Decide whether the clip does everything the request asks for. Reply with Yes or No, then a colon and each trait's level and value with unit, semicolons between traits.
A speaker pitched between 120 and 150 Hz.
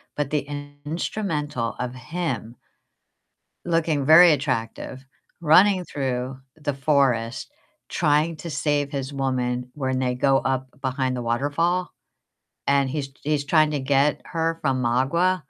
Yes: medium, 140 Hz